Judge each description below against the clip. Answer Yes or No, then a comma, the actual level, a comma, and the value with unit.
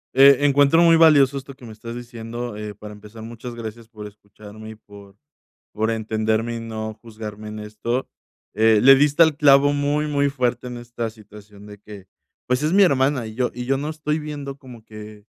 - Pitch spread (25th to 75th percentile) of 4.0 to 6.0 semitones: Yes, average, 4.4 semitones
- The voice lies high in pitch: No, low, 120 Hz